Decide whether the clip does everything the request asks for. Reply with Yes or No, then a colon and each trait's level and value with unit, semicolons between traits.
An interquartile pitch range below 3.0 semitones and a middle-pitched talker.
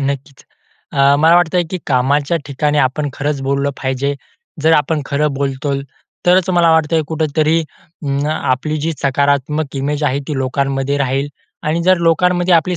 Yes: narrow, 2.6 semitones; medium, 145 Hz